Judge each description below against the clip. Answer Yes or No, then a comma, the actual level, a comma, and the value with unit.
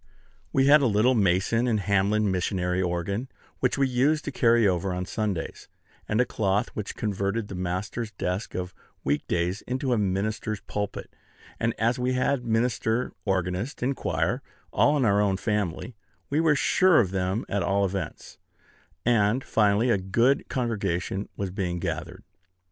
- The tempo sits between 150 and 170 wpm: Yes, average, 160 wpm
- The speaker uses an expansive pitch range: No, average, 4.3 semitones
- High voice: No, low, 105 Hz